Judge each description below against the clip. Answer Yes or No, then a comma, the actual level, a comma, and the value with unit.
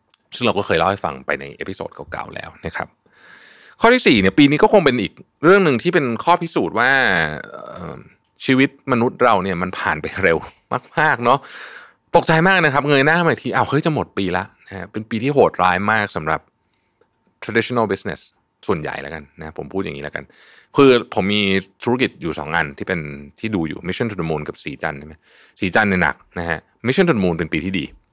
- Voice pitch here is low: Yes, low, 110 Hz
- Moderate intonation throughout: No, wide, 8.0 semitones